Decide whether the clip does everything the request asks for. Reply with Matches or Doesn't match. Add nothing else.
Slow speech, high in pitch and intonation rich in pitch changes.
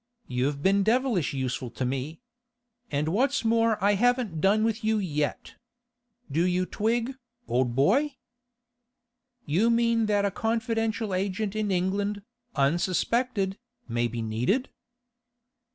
Matches